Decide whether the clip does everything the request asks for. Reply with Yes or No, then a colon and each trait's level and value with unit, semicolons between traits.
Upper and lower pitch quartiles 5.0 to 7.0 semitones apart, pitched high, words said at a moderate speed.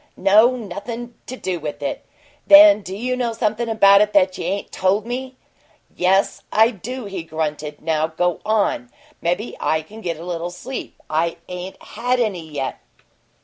Yes: wide, 5.5 semitones; high, 200 Hz; average, 170 wpm